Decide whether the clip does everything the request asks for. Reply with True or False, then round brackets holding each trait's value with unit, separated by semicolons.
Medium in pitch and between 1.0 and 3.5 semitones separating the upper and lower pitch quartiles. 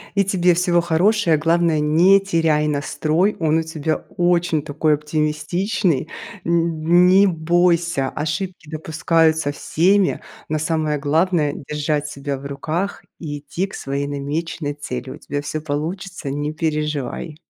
True (160 Hz; 2.7 semitones)